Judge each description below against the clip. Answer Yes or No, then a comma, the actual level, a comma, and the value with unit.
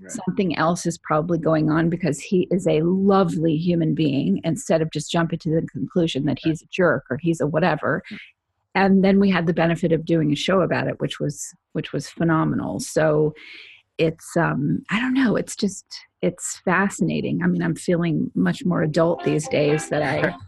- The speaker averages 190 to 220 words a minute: Yes, average, 195 wpm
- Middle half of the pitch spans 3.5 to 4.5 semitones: No, average, 2.9 semitones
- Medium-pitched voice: Yes, medium, 165 Hz